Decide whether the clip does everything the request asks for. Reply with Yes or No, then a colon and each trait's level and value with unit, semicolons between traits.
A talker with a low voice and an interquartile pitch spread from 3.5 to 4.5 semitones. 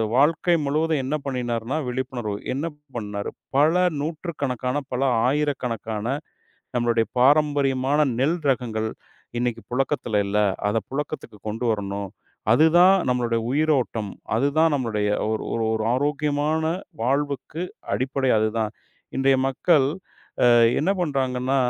Yes: low, 130 Hz; average, 4.2 semitones